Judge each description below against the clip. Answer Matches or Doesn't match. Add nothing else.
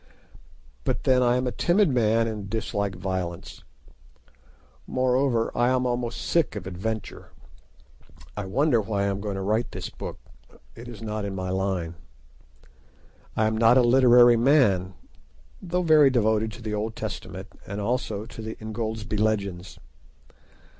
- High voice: Doesn't match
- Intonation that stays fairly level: Doesn't match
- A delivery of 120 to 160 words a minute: Matches